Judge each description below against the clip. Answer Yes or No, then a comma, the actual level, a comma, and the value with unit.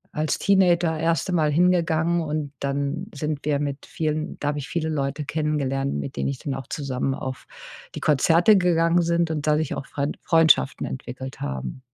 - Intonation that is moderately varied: Yes, average, 3.0 semitones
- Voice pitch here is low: No, medium, 150 Hz